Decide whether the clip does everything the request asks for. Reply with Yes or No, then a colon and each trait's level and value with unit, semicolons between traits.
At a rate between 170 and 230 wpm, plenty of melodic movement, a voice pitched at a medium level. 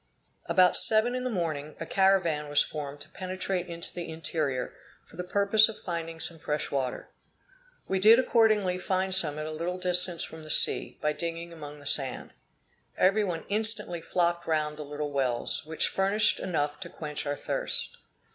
No: average, 175 wpm; average, 4.0 semitones; medium, 170 Hz